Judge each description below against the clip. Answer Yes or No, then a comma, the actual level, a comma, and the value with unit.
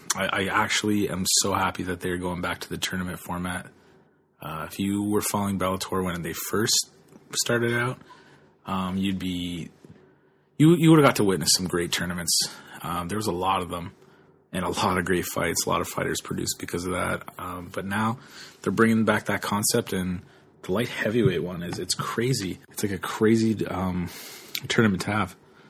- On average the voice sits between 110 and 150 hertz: No, very low, 95 Hz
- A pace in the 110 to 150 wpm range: No, average, 190 wpm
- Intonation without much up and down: No, average, 3.2 semitones